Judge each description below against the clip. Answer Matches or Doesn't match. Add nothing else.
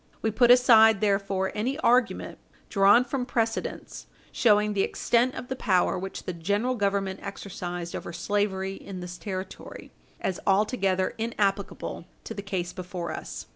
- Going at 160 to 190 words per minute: Doesn't match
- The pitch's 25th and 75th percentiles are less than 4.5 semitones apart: Matches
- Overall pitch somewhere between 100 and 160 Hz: Doesn't match